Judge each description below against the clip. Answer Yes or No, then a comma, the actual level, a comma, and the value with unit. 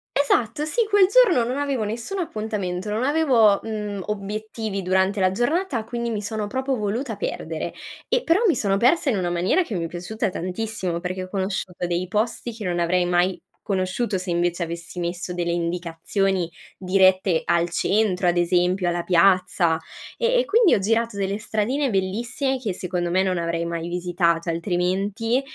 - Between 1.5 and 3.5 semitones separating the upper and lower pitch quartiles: No, average, 4.5 semitones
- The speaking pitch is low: No, high, 195 Hz